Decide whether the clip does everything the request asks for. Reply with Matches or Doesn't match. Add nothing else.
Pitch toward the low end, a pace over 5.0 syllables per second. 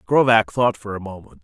Matches